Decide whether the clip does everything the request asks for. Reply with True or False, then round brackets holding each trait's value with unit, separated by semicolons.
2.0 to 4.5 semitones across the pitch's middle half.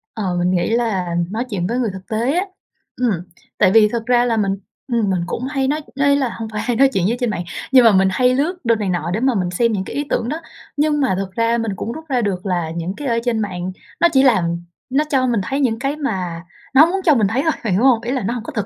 False (5.4 semitones)